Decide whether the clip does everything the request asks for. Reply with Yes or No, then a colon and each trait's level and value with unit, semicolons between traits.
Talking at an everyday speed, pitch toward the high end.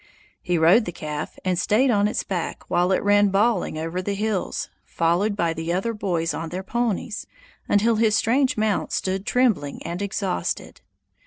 Yes: average, 170 wpm; high, 195 Hz